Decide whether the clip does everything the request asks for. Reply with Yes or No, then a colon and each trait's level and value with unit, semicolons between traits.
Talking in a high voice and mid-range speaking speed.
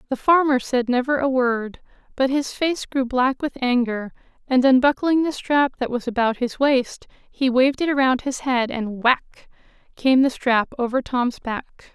Yes: very high, 255 Hz; average, 180 wpm